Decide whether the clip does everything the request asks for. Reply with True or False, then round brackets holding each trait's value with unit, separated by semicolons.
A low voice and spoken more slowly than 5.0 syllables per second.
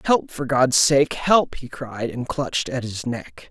True (130 Hz; 3.9 syllables/s)